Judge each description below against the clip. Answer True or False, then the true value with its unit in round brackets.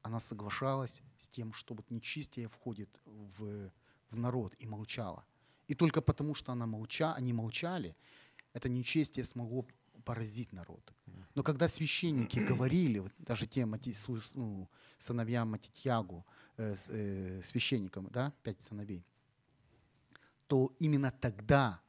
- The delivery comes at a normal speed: True (120 wpm)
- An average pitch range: True (3.6 semitones)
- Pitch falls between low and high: False (120 Hz)